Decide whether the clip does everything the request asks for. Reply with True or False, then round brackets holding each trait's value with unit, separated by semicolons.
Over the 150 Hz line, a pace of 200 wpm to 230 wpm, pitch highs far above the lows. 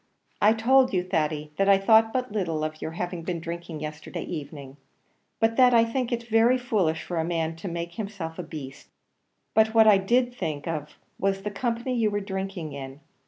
True (190 Hz; 205 wpm; 5.7 semitones)